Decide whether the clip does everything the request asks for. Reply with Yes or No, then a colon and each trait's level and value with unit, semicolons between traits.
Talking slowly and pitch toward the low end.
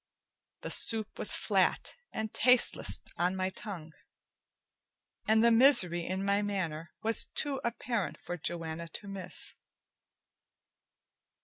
No: slow, 115 wpm; high, 195 Hz